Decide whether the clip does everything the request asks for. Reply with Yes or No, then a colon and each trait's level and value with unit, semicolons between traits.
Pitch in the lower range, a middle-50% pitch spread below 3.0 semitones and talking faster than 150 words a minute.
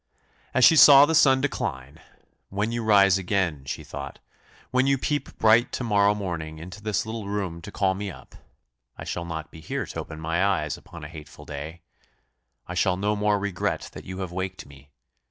No: very low, 95 Hz; average, 4.5 semitones; average, 195 wpm